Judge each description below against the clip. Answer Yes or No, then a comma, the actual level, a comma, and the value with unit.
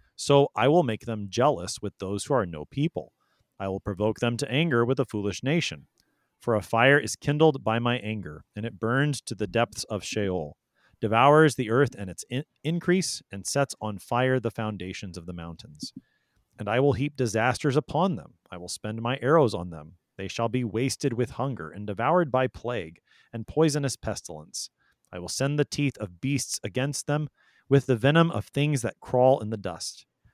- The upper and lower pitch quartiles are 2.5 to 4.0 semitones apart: No, average, 5.3 semitones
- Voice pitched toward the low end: Yes, low, 120 Hz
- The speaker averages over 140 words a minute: Yes, average, 200 wpm